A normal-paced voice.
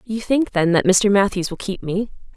No: fast, 230 wpm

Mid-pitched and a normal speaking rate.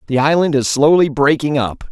Yes: medium, 145 Hz; average, 190 wpm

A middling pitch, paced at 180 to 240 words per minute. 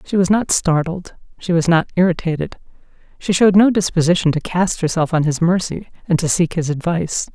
Yes: medium, 170 Hz; average, 190 wpm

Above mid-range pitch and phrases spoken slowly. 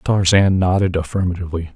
No: very low, 90 Hz; slow, 100 wpm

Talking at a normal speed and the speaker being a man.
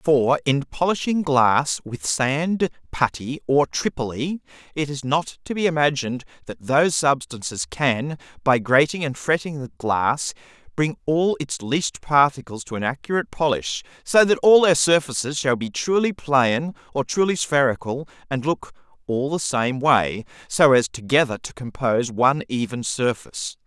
Yes: average, 150 wpm; male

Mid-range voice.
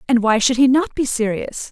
No: very high, 250 Hz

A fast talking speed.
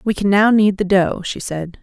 Yes: fast, 265 wpm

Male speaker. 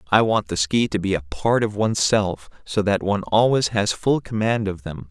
Yes: male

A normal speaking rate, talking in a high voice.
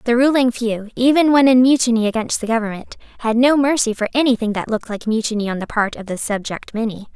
No: fast, 225 wpm; high, 230 Hz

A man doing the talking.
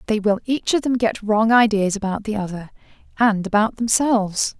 No: female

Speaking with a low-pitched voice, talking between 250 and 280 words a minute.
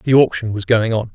Yes: low, 115 Hz; fast, 265 wpm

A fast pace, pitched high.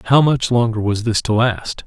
No: fast, 225 wpm; low, 115 Hz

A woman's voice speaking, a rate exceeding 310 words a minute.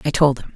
Yes: female; fast, 325 wpm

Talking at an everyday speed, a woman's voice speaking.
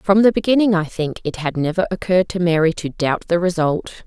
No: fast, 220 wpm; female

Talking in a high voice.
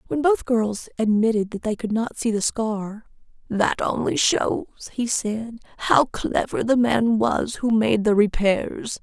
Yes: high, 220 Hz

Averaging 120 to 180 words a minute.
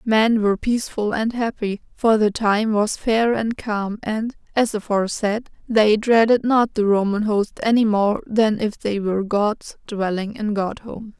Yes: average, 170 wpm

